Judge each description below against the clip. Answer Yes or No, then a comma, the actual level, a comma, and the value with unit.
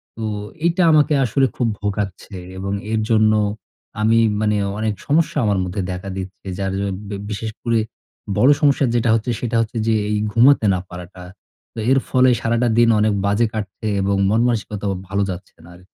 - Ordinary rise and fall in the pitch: Yes, average, 3.1 semitones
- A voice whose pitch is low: Yes, low, 110 Hz